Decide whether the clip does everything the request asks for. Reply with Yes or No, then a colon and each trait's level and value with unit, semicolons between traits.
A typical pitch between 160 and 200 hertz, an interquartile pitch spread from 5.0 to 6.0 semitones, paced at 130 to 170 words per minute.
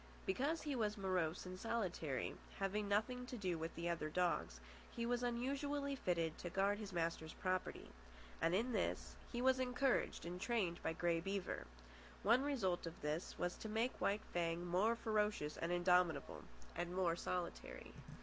Yes: high, 190 Hz; wide, 5.4 semitones; average, 165 wpm